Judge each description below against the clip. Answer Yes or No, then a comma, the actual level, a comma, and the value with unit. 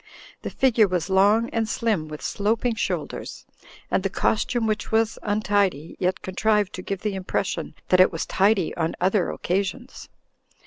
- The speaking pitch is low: No, high, 200 Hz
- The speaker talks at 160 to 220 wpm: Yes, average, 165 wpm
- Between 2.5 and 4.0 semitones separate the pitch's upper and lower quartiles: Yes, average, 3.2 semitones